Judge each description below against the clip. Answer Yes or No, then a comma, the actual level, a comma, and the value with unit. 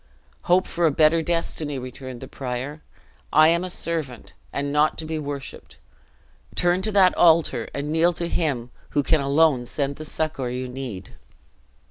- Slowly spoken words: No, average, 165 wpm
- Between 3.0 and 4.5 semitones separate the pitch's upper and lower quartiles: Yes, average, 3.8 semitones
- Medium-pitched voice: Yes, medium, 150 Hz